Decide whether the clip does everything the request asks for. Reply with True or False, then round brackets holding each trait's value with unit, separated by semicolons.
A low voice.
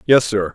True (115 Hz)